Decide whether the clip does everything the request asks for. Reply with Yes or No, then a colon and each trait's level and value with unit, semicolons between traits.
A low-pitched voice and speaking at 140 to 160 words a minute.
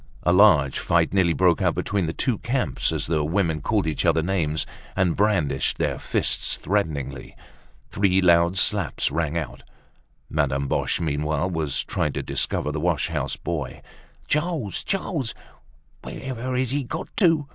Yes: very low, 85 Hz; average, 155 wpm